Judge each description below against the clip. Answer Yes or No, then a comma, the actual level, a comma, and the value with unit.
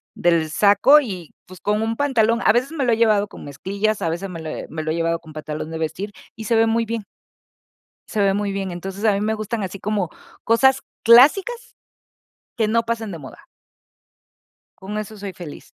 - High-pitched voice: Yes, high, 205 Hz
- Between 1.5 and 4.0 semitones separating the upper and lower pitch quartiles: No, average, 4.6 semitones